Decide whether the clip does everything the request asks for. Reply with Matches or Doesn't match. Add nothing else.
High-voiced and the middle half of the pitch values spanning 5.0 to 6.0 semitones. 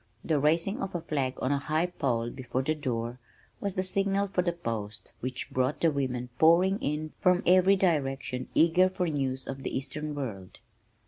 Doesn't match